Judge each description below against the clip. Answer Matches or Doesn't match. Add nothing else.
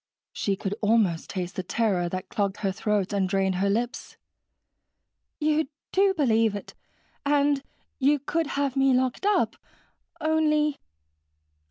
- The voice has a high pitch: Matches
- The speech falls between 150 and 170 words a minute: Doesn't match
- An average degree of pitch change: Doesn't match